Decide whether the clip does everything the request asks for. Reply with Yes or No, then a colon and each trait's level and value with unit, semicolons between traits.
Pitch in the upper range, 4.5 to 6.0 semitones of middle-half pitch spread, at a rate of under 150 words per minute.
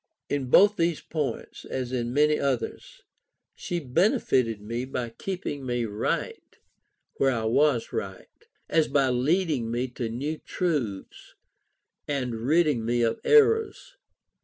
No: low, 135 Hz; average, 5.0 semitones; slow, 135 wpm